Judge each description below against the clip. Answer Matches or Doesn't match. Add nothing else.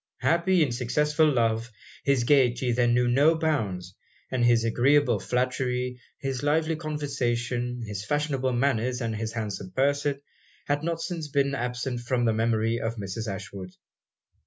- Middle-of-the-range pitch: Doesn't match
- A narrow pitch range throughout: Doesn't match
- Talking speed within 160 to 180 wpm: Doesn't match